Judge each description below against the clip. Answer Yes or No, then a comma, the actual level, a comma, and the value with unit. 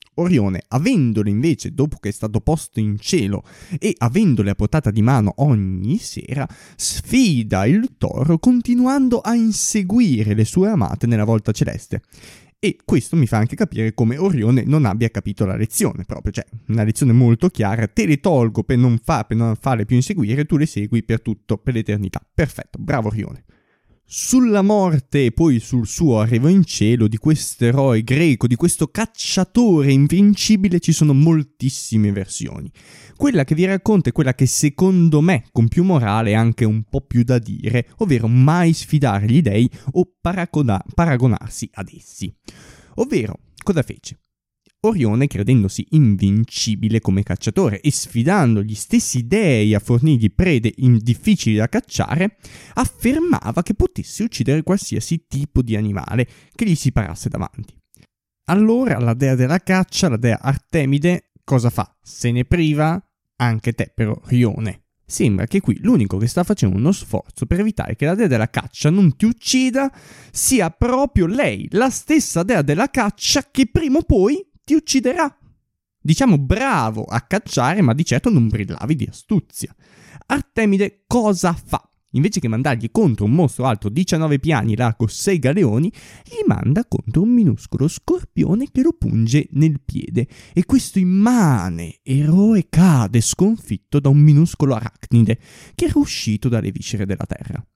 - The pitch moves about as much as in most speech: No, wide, 7.9 semitones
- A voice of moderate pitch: No, low, 130 Hz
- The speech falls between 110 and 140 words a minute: No, average, 155 wpm